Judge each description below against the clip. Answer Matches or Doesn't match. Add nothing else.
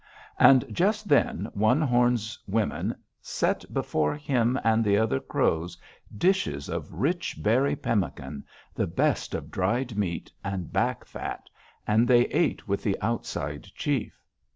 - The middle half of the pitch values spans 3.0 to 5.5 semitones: Matches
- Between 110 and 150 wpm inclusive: Matches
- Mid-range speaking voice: Doesn't match